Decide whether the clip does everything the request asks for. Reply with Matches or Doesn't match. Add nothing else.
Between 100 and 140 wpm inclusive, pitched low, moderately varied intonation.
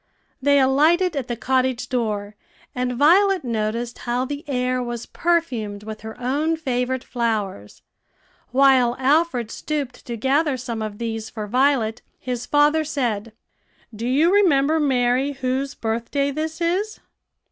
Doesn't match